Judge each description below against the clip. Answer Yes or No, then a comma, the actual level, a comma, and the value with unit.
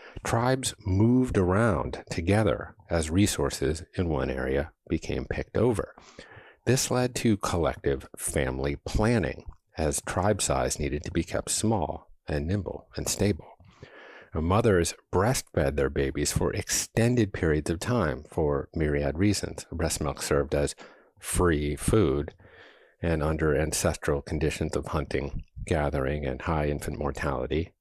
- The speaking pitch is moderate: No, very low, 80 Hz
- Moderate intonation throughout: No, wide, 5.7 semitones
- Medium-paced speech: No, slow, 125 wpm